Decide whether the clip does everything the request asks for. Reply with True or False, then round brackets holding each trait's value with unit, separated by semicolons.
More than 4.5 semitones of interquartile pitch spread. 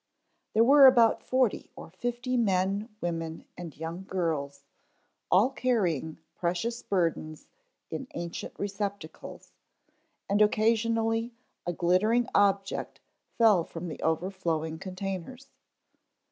True (5.2 semitones)